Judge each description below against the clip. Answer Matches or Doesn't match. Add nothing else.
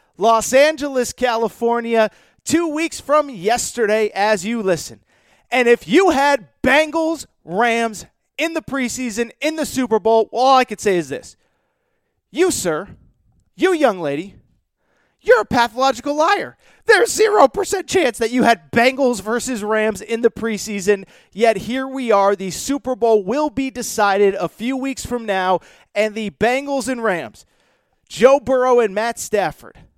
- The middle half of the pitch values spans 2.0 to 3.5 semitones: Doesn't match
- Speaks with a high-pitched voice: Matches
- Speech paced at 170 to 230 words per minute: Doesn't match